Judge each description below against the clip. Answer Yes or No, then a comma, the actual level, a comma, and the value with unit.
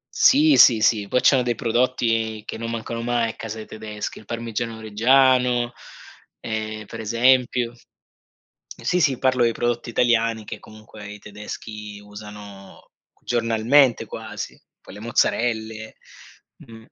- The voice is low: Yes, low, 115 Hz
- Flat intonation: Yes, narrow, 2.0 semitones